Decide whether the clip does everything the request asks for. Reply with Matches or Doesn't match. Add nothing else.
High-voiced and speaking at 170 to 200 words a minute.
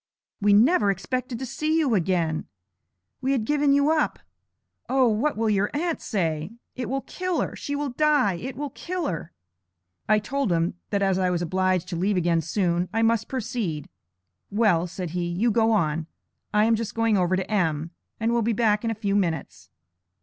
Matches